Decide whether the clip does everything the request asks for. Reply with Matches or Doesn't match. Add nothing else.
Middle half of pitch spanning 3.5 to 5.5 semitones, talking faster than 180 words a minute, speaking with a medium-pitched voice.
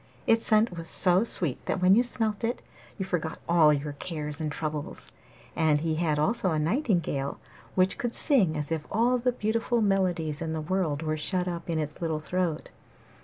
Matches